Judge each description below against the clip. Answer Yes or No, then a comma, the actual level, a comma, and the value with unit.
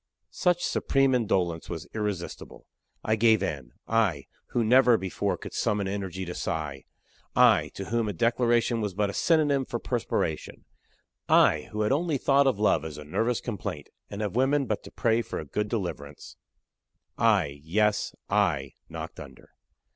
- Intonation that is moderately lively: Yes, average, 4.9 semitones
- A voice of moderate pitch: No, low, 105 Hz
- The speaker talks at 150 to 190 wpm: Yes, average, 160 wpm